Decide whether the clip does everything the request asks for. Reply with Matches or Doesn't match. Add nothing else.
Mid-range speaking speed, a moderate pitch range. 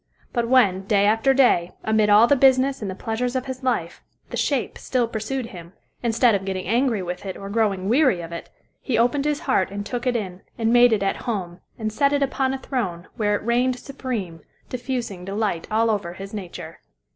Doesn't match